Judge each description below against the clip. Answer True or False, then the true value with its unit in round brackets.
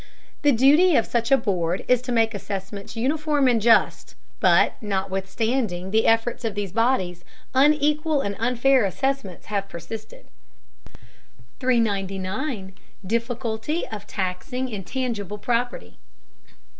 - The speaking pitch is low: False (225 Hz)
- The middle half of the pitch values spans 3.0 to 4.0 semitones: False (4.7 semitones)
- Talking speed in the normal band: False (115 wpm)